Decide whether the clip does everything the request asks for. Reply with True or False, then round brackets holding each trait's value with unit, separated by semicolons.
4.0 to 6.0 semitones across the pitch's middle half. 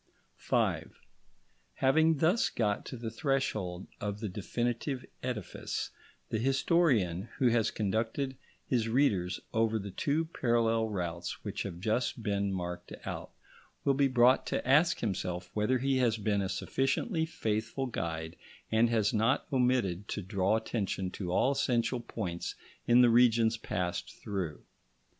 True (4.5 semitones)